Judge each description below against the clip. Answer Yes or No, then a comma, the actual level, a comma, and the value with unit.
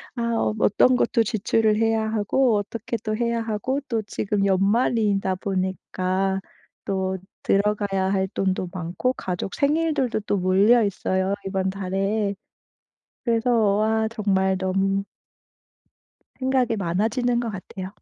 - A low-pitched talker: No, high, 205 Hz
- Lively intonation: No, average, 3.2 semitones